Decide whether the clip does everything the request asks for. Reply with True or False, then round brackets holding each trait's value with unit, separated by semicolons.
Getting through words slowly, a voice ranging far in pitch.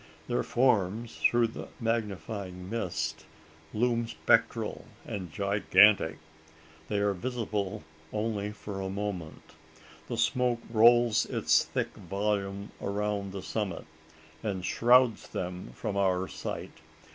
False (110 wpm; 3.1 semitones)